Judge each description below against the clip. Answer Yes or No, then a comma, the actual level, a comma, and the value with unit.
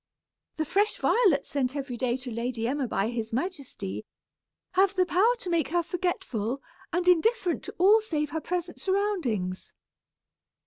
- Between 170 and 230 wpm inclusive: No, average, 150 wpm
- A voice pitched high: Yes, very high, 315 Hz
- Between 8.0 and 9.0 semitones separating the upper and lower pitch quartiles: No, wide, 6.9 semitones